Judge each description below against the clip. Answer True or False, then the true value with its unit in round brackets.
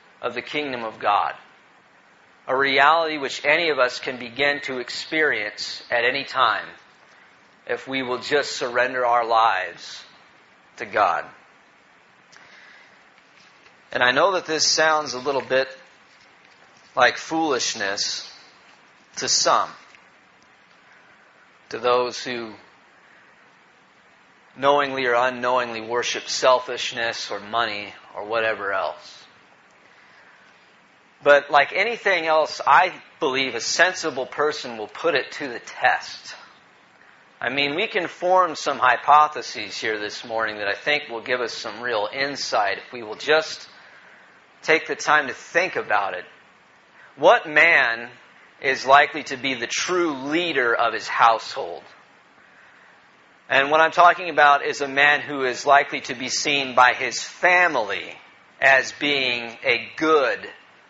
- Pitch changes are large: False (3.6 semitones)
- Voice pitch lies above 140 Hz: False (135 Hz)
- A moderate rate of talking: False (130 wpm)